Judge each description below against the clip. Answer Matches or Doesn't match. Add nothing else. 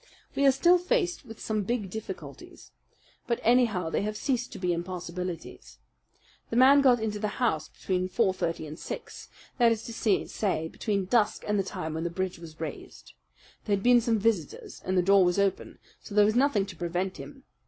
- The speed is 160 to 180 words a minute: Doesn't match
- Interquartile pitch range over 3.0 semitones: Matches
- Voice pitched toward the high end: Matches